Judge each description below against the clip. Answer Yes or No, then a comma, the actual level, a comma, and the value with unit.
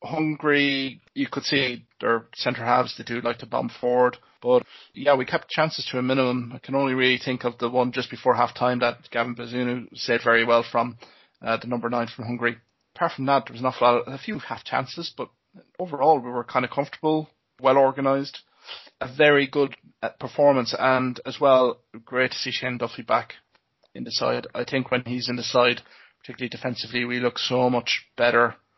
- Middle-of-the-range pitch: No, low, 125 Hz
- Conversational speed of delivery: Yes, average, 195 wpm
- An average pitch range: No, narrow, 2.2 semitones